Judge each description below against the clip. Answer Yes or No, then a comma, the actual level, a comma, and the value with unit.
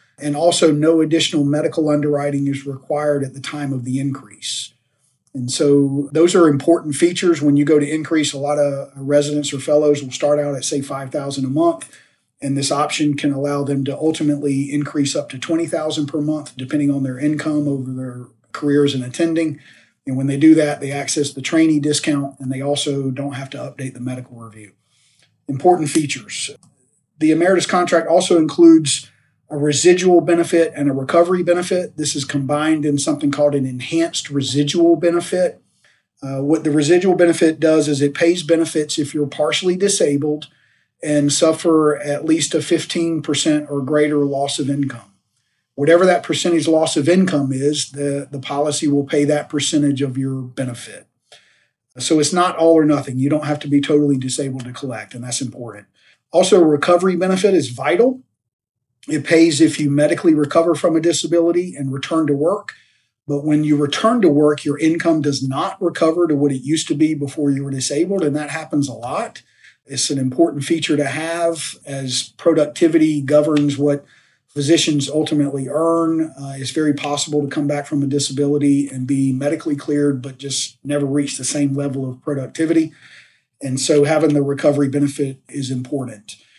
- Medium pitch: Yes, medium, 145 Hz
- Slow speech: No, average, 175 wpm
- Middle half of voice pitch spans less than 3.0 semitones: Yes, narrow, 2.4 semitones